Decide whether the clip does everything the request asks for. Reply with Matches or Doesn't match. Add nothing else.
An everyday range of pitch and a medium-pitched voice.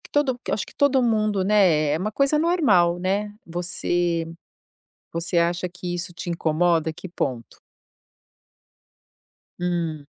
Matches